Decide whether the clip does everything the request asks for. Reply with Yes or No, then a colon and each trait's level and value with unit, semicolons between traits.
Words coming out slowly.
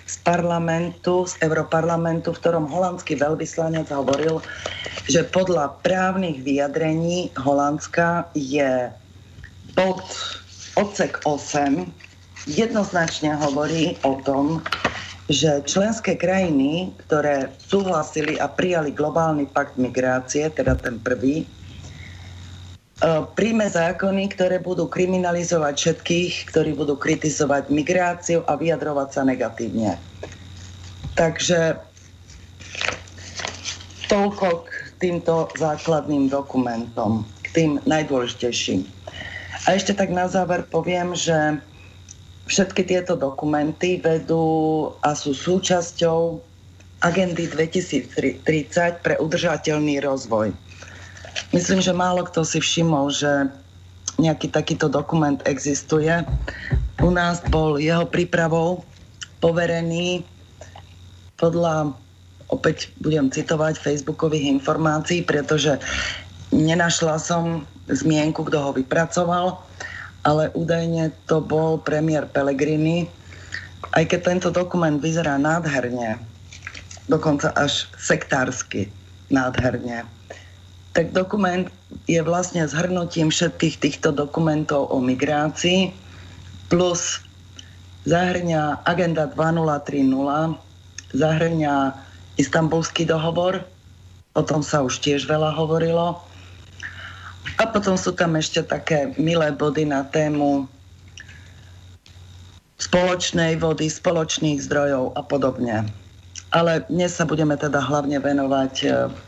Yes: slow, 95 wpm